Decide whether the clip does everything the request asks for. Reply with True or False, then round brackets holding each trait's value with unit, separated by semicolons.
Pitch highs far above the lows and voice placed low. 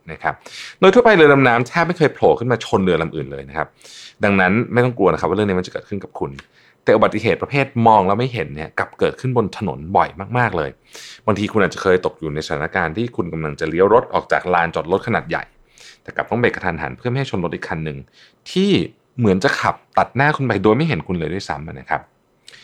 True (8.1 semitones; 110 Hz)